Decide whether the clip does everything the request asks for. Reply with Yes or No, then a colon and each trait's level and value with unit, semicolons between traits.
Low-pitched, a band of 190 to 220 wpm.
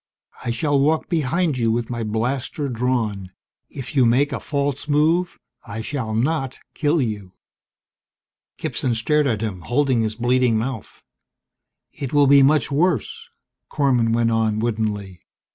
No: low, 125 Hz; average, 145 wpm